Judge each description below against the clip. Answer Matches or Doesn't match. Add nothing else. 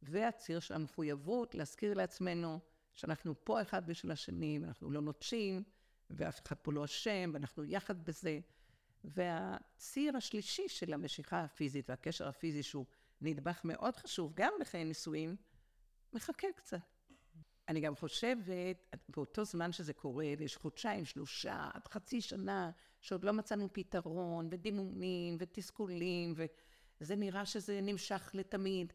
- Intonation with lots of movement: Doesn't match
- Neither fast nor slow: Matches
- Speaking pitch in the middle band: Matches